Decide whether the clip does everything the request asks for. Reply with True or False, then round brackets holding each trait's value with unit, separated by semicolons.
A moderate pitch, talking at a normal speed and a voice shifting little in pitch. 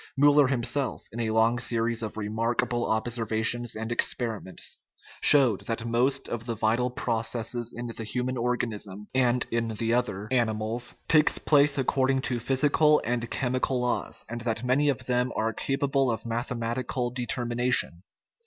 False (120 Hz; 150 wpm; 2.0 semitones)